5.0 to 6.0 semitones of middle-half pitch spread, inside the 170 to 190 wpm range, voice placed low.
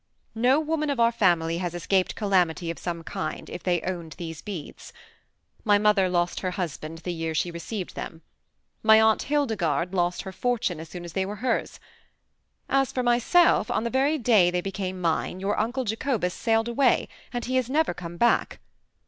No: average, 5.3 semitones; average, 185 wpm; high, 195 Hz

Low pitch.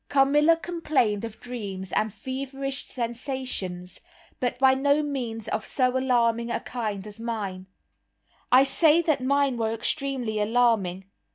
No: high, 245 Hz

